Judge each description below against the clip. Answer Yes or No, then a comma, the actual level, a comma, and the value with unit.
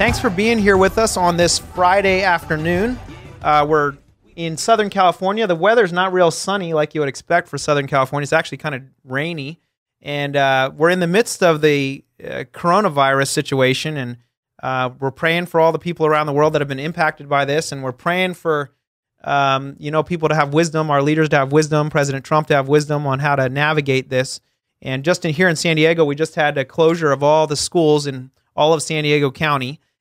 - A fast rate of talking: Yes, fast, 215 wpm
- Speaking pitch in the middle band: Yes, medium, 150 Hz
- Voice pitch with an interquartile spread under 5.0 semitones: Yes, average, 3.2 semitones